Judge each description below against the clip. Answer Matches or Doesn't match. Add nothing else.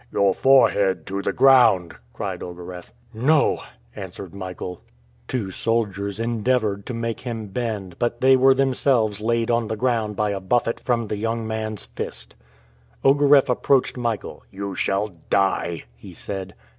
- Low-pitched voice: Matches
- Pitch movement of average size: Matches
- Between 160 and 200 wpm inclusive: Doesn't match